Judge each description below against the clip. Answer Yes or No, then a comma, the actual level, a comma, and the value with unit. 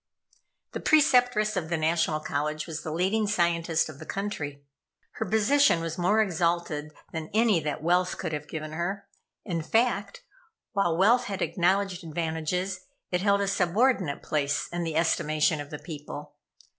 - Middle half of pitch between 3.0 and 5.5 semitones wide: Yes, average, 4.2 semitones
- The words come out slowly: No, average, 155 wpm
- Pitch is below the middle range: No, medium, 170 Hz